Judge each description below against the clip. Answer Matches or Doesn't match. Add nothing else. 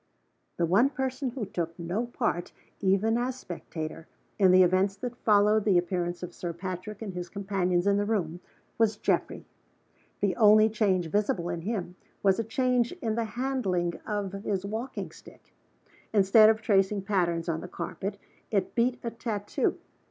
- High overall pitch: Matches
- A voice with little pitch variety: Doesn't match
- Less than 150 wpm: Doesn't match